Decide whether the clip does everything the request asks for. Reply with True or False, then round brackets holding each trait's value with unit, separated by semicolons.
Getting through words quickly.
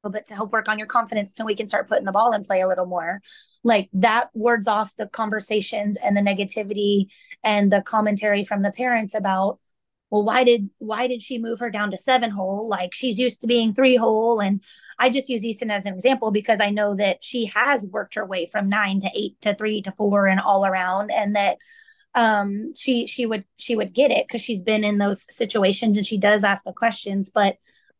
True (225 wpm)